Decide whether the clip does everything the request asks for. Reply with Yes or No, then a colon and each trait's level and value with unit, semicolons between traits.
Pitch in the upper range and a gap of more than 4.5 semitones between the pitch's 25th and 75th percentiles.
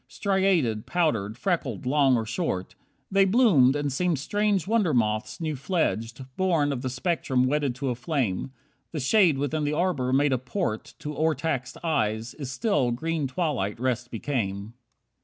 No: medium, 140 Hz; average, 5.2 semitones